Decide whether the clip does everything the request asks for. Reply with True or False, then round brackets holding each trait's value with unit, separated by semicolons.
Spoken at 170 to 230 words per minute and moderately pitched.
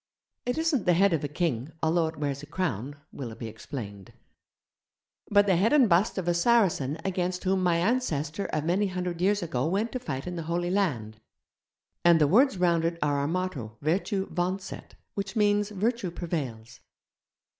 True (180 wpm; 175 Hz)